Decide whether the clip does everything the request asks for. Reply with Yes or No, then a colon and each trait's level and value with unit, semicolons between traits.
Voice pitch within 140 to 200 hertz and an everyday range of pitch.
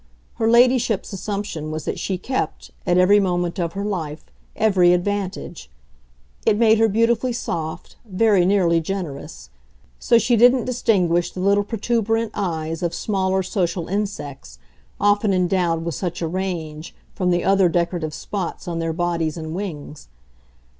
Yes: medium, 185 Hz; average, 3.7 semitones